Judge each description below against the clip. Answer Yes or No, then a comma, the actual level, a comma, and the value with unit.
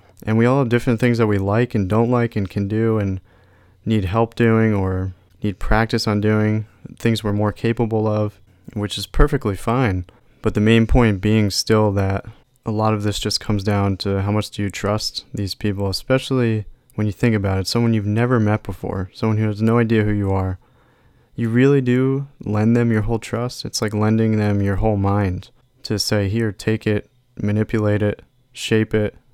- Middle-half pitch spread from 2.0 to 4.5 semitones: Yes, narrow, 2.4 semitones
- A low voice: Yes, low, 110 Hz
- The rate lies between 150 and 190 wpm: No, average, 200 wpm